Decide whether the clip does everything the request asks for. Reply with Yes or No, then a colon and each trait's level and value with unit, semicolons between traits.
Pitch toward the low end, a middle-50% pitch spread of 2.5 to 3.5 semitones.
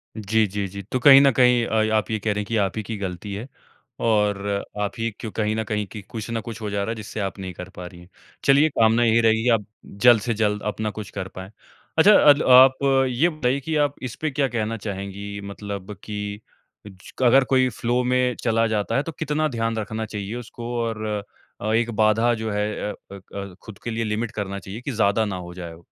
Yes: low, 110 Hz; average, 2.8 semitones